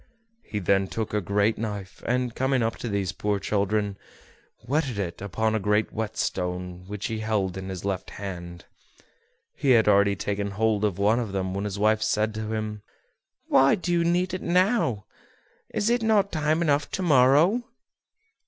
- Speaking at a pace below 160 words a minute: No, average, 180 wpm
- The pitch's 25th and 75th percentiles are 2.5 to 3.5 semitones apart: No, average, 4.7 semitones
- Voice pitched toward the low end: Yes, low, 110 Hz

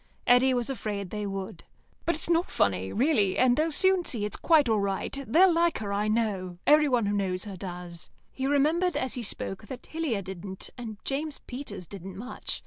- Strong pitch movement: Yes, wide, 6.7 semitones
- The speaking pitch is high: Yes, high, 225 Hz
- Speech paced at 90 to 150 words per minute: No, average, 195 wpm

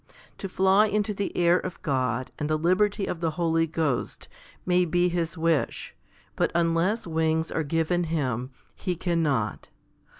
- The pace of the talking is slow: No, average, 155 wpm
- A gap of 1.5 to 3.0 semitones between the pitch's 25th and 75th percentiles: Yes, narrow, 2.4 semitones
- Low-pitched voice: No, medium, 165 Hz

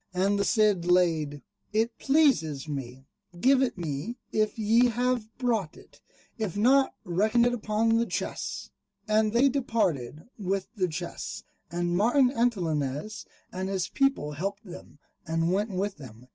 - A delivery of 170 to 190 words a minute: No, average, 145 wpm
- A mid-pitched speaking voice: No, high, 200 Hz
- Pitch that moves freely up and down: Yes, wide, 5.8 semitones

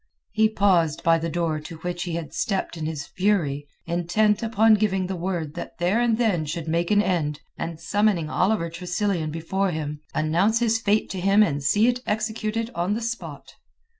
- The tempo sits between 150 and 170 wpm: No, average, 190 wpm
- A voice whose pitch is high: No, medium, 180 Hz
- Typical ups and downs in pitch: Yes, average, 4.5 semitones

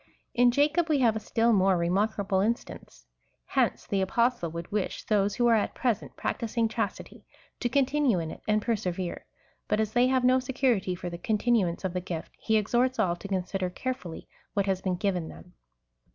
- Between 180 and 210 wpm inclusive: Yes, average, 185 wpm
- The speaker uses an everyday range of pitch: Yes, average, 4.7 semitones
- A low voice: No, high, 210 Hz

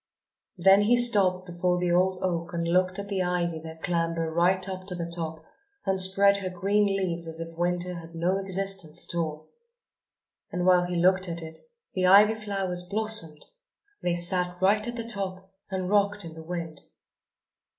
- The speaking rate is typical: Yes, average, 180 wpm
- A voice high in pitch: No, medium, 180 Hz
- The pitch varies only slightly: Yes, narrow, 2.3 semitones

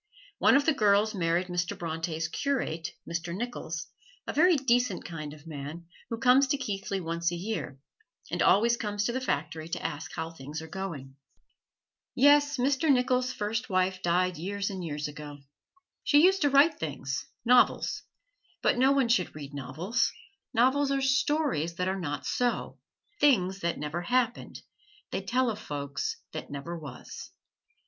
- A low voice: No, high, 190 Hz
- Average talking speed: Yes, average, 160 wpm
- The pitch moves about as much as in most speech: No, wide, 7.6 semitones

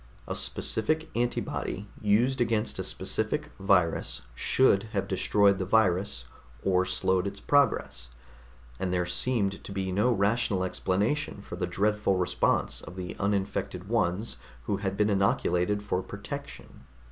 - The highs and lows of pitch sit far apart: No, average, 2.7 semitones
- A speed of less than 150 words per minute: Yes, slow, 135 wpm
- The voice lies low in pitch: Yes, low, 100 Hz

